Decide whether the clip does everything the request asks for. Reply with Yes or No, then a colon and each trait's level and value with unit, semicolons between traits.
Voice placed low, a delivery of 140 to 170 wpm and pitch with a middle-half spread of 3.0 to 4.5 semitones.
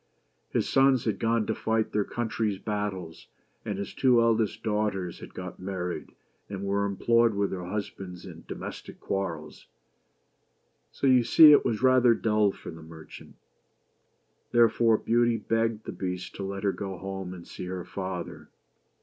Yes: low, 105 Hz; average, 160 wpm; average, 3.3 semitones